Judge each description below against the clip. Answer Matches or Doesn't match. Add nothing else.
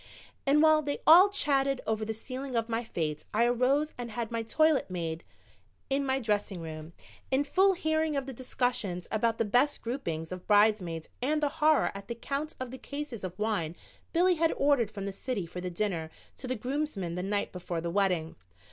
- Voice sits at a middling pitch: Doesn't match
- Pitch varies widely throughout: Matches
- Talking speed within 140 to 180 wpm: Doesn't match